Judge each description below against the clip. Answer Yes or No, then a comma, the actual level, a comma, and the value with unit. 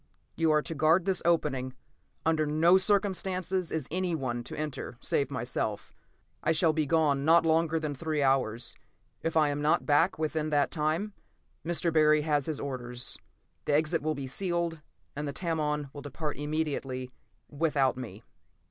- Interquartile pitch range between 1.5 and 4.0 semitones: Yes, average, 2.7 semitones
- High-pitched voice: No, medium, 155 Hz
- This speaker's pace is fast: No, average, 160 wpm